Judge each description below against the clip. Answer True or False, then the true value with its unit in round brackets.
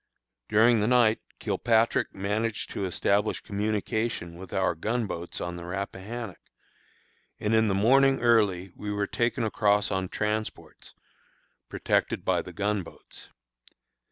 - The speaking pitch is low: True (105 Hz)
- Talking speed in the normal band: False (130 wpm)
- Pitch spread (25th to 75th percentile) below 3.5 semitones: True (2.6 semitones)